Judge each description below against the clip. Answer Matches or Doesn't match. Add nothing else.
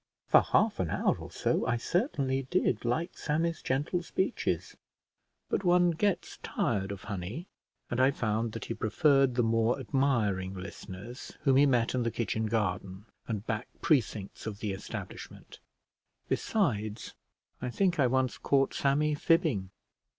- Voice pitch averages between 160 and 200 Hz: Doesn't match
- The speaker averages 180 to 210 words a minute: Doesn't match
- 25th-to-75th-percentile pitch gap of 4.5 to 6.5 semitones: Matches